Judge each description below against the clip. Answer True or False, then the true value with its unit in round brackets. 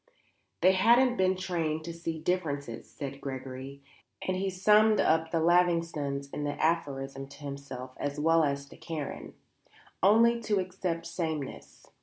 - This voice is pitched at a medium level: True (160 Hz)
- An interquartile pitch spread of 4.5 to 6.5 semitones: True (4.8 semitones)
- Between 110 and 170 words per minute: True (145 wpm)